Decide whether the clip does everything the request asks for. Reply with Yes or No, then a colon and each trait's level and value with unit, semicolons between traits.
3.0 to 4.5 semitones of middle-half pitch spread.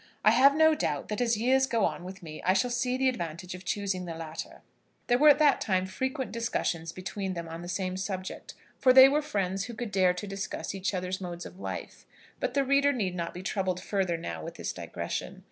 No: wide, 5.5 semitones